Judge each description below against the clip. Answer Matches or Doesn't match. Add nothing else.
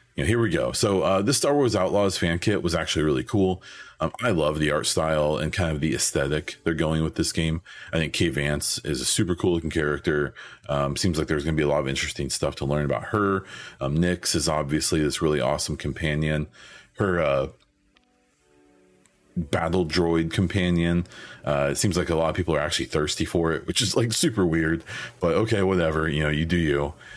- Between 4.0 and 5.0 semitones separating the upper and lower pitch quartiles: Doesn't match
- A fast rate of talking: Matches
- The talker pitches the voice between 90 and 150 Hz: Doesn't match